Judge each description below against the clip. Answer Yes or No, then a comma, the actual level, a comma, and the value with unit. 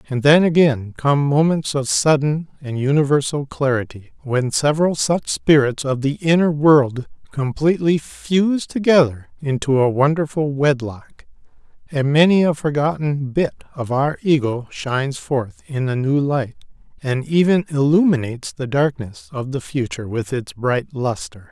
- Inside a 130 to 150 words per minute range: Yes, average, 140 wpm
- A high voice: No, medium, 140 Hz